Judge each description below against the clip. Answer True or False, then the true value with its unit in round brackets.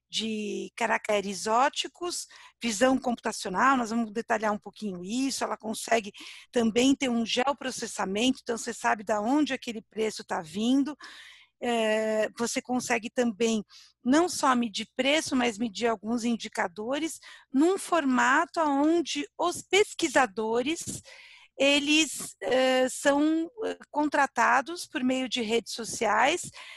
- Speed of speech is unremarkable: False (110 wpm)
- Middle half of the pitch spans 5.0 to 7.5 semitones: False (4.2 semitones)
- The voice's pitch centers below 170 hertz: False (245 Hz)